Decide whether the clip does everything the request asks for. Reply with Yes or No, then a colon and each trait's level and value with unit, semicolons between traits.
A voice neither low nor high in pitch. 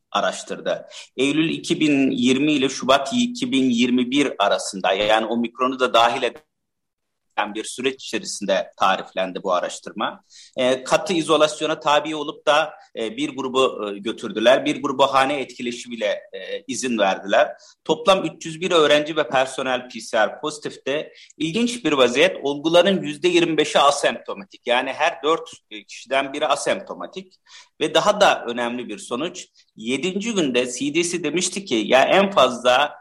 Yes: medium, 150 Hz